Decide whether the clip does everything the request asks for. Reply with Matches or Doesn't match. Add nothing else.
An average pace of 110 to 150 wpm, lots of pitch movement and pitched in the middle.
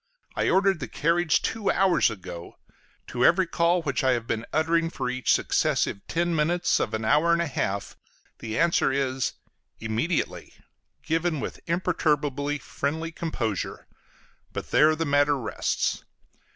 Doesn't match